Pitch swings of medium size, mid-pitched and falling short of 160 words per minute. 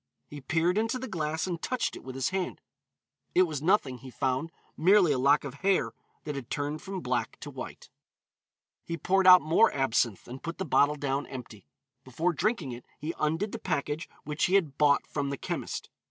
No: average, 4.8 semitones; medium, 155 Hz; average, 200 wpm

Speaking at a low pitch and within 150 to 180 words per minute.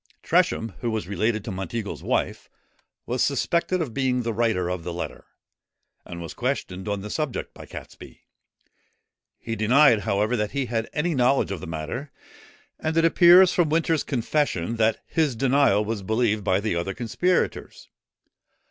Yes: low, 115 Hz; average, 160 wpm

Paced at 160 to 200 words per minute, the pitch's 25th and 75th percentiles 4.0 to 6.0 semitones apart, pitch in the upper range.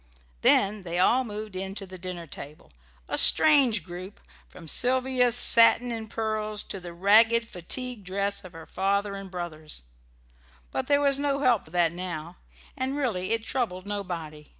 Yes: average, 165 wpm; average, 4.6 semitones; high, 200 Hz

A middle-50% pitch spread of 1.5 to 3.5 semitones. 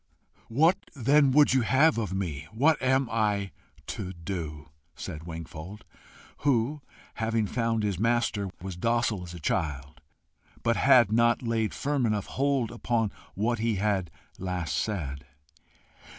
No: average, 4.8 semitones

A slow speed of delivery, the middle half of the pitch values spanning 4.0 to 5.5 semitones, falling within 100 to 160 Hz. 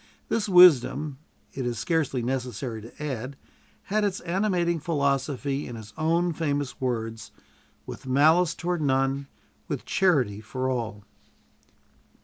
Yes: slow, 125 wpm; average, 5.1 semitones; medium, 140 Hz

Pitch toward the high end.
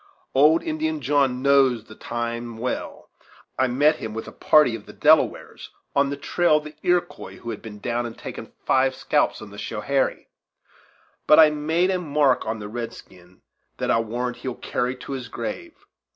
No: low, 130 Hz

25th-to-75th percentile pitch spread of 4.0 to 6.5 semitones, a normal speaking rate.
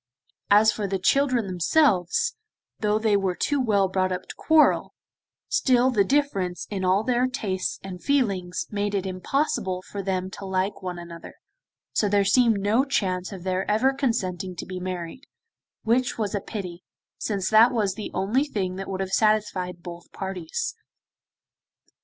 No: average, 3.6 semitones; average, 165 wpm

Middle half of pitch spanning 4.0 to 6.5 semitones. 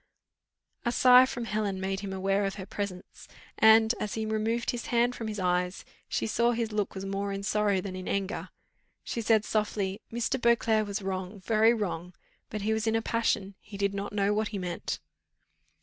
No: narrow, 2.4 semitones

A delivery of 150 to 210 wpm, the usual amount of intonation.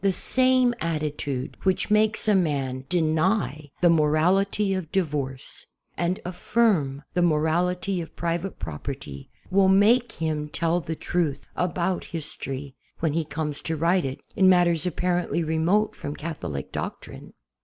No: average, 140 wpm; average, 3.8 semitones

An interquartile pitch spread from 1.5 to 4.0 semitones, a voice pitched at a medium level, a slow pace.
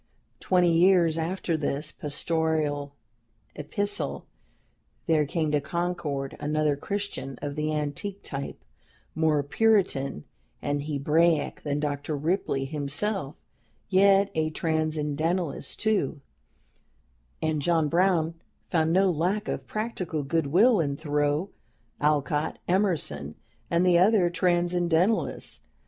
Yes: average, 3.6 semitones; medium, 160 Hz; slow, 105 wpm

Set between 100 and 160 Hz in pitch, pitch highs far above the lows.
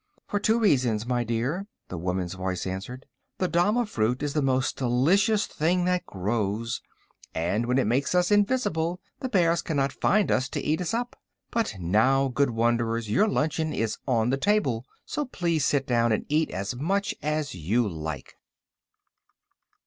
Yes: low, 135 Hz; wide, 7.7 semitones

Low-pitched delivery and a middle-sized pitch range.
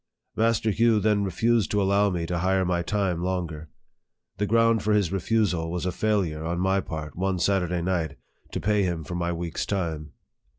Yes: very low, 95 Hz; average, 3.2 semitones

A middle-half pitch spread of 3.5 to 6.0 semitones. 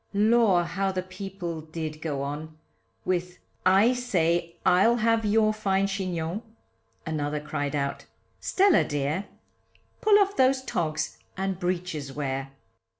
Yes: average, 4.9 semitones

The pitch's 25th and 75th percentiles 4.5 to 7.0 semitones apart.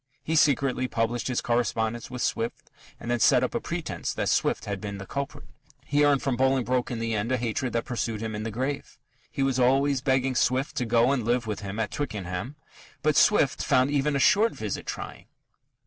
No: average, 3.0 semitones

